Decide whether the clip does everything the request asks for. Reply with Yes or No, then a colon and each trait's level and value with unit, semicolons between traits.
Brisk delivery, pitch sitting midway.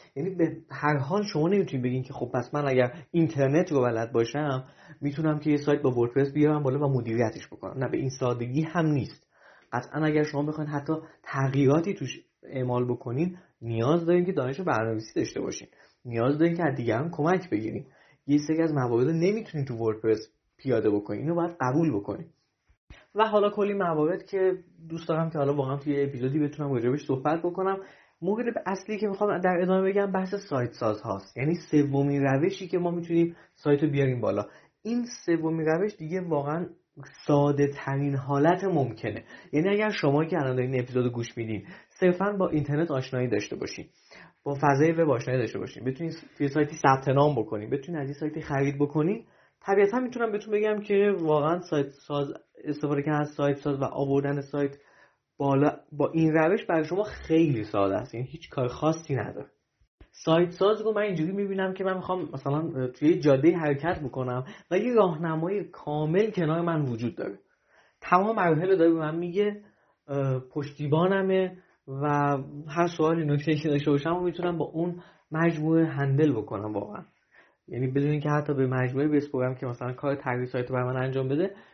Yes: fast, 175 wpm; medium, 150 Hz